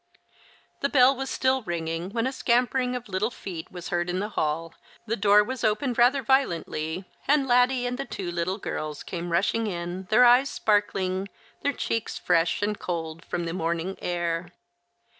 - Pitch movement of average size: No, wide, 6.2 semitones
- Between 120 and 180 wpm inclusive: Yes, average, 175 wpm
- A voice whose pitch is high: Yes, high, 200 Hz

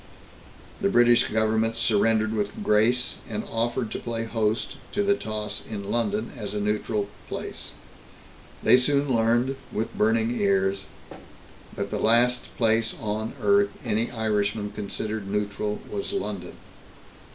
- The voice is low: Yes, low, 110 Hz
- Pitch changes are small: Yes, narrow, 2.1 semitones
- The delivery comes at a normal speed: No, slow, 130 wpm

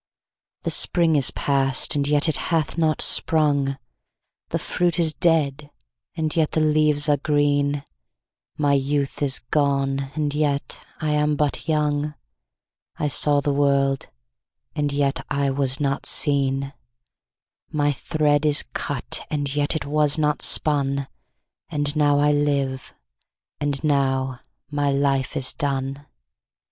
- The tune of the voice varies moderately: No, narrow, 1.5 semitones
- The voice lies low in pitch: No, medium, 145 Hz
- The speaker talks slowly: Yes, slow, 125 wpm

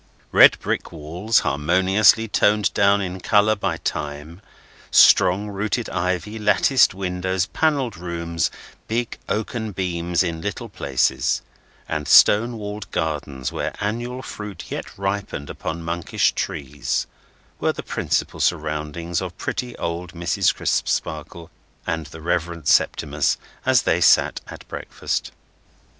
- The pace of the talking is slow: Yes, slow, 120 wpm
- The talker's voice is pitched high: No, very low, 90 Hz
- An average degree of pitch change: Yes, average, 4.3 semitones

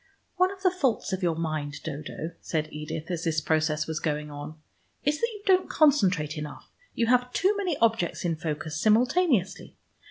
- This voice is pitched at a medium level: Yes, medium, 170 Hz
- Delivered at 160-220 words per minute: Yes, average, 180 wpm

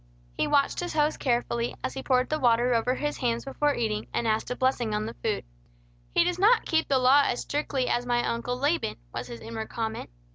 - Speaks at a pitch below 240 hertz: No, very high, 250 Hz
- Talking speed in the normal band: No, fast, 220 wpm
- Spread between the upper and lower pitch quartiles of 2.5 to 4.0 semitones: Yes, average, 3.7 semitones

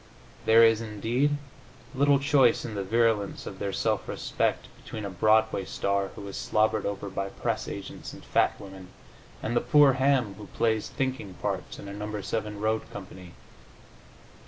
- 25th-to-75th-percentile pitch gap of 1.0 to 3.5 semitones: Yes, average, 2.7 semitones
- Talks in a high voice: No, low, 110 Hz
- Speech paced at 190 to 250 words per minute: No, average, 165 wpm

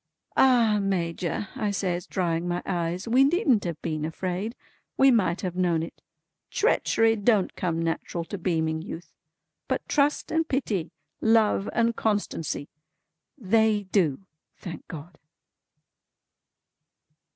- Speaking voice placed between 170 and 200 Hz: Yes, high, 190 Hz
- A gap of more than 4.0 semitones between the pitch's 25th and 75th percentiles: Yes, average, 5.0 semitones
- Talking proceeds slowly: Yes, slow, 120 wpm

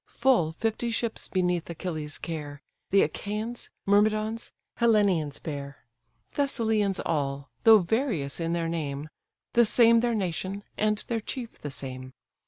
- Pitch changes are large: Yes, wide, 6.4 semitones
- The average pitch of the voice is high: Yes, high, 195 Hz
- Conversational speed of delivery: No, slow, 130 wpm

